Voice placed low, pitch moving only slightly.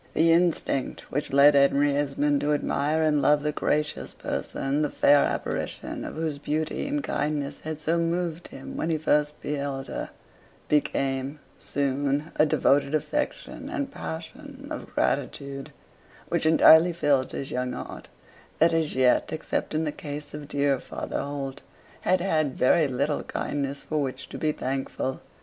No: medium, 150 Hz; narrow, 2.2 semitones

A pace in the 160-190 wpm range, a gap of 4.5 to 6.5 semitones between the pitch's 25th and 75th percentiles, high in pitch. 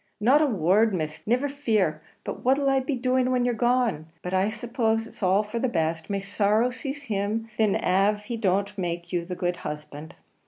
No: average, 200 wpm; average, 5.2 semitones; high, 215 Hz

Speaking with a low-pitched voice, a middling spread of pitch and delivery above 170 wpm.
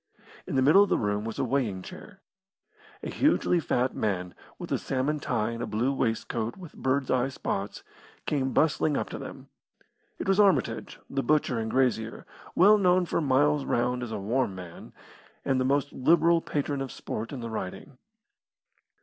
Yes: low, 130 Hz; average, 4.8 semitones; average, 180 wpm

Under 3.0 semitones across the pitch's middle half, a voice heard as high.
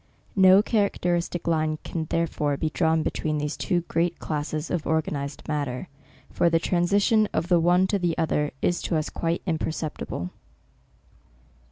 No: narrow, 2.4 semitones; medium, 165 Hz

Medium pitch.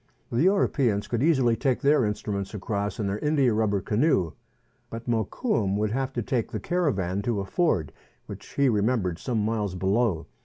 No: low, 110 Hz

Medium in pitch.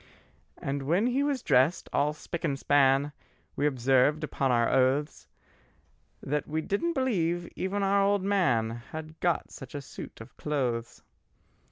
Yes: medium, 150 Hz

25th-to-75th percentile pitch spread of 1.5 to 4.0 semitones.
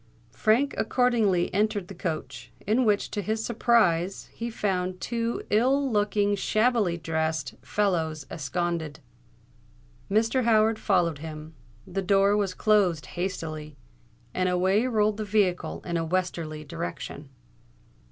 No: average, 4.8 semitones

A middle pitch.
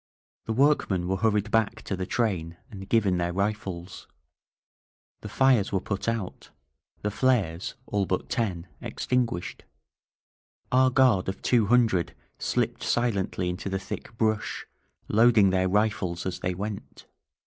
No: low, 100 Hz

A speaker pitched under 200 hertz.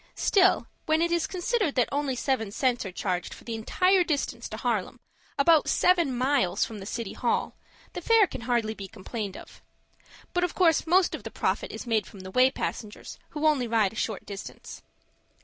No: very high, 255 Hz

